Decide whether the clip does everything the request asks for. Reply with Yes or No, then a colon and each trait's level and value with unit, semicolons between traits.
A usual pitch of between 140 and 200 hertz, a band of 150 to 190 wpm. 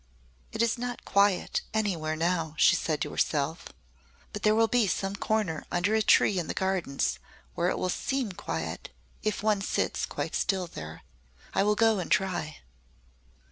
Yes: high, 190 Hz; average, 170 wpm